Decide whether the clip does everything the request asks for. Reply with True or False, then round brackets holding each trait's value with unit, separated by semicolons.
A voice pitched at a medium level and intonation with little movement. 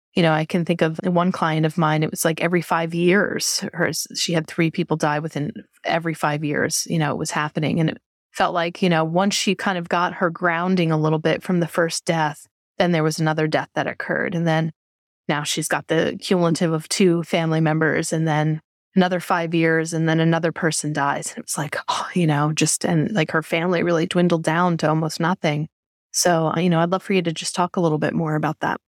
True (165 Hz; 2.0 semitones)